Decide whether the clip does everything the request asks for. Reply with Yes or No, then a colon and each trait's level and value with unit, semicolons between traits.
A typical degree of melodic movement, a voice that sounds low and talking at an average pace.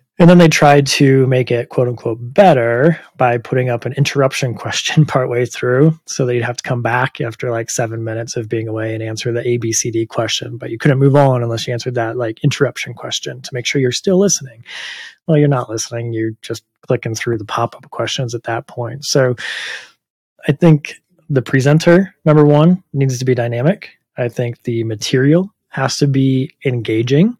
Yes: average, 3.5 semitones; low, 125 Hz; average, 195 wpm